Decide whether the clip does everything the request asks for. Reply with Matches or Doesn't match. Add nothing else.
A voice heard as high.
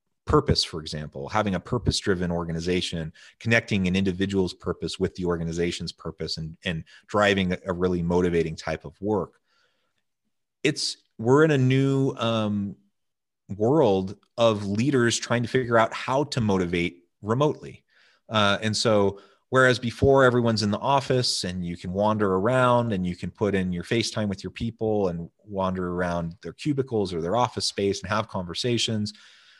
Doesn't match